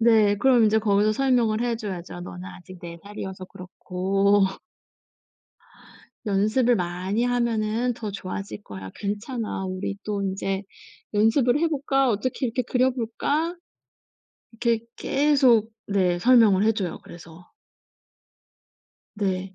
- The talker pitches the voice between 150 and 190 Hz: No, high, 215 Hz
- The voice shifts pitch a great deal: No, average, 4.0 semitones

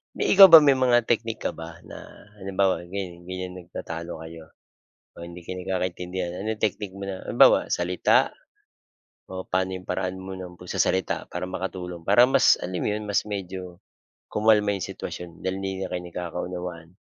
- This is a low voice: Yes, very low, 95 Hz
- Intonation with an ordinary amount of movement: No, narrow, 1.7 semitones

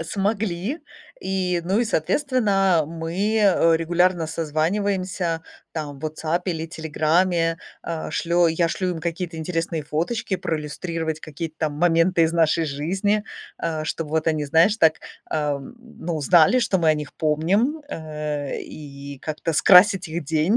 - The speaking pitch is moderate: Yes, medium, 165 Hz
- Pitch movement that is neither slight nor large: Yes, average, 3.0 semitones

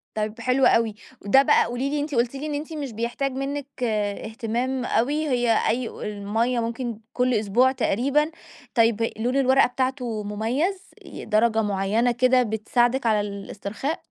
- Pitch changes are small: No, average, 3.3 semitones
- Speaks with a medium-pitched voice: No, high, 245 Hz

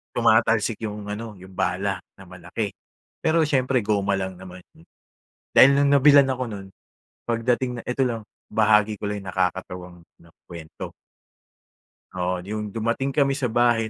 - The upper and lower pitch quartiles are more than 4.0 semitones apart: Yes, average, 4.7 semitones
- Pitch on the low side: Yes, low, 105 Hz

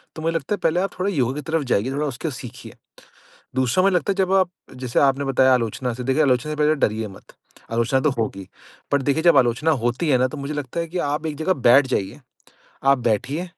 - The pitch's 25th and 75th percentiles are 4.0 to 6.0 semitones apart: Yes, average, 4.3 semitones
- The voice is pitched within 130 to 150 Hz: Yes, medium, 140 Hz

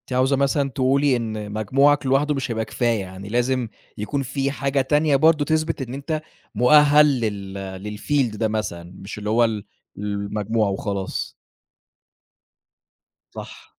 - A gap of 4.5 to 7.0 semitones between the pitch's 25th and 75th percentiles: Yes, average, 4.9 semitones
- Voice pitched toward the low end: Yes, low, 120 Hz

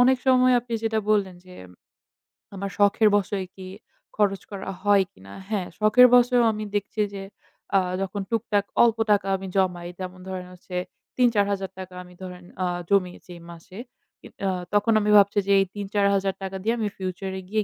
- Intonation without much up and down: Yes, narrow, 2.3 semitones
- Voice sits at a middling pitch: No, high, 200 Hz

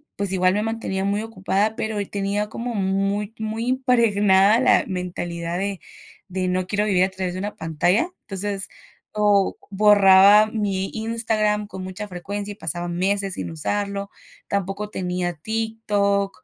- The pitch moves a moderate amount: No, narrow, 1.9 semitones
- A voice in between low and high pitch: No, high, 200 Hz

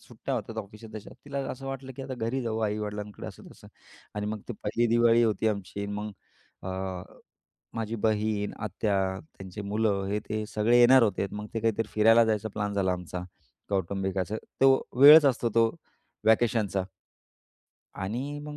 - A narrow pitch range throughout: Yes, narrow, 2.3 semitones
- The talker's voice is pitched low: Yes, low, 110 Hz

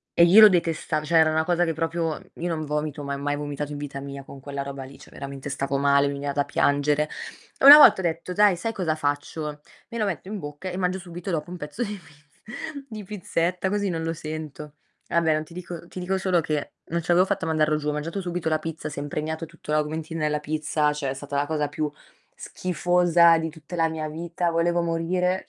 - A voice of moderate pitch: Yes, medium, 160 Hz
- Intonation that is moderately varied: Yes, average, 3.0 semitones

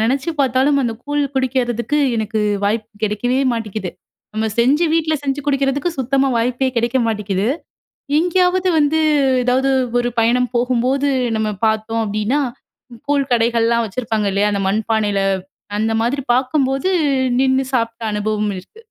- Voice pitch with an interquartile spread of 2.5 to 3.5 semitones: No, average, 3.9 semitones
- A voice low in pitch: No, high, 240 Hz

